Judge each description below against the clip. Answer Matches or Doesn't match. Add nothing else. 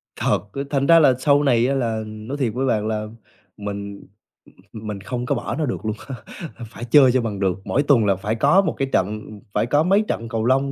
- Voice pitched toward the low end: Matches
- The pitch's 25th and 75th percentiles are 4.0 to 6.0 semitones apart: Matches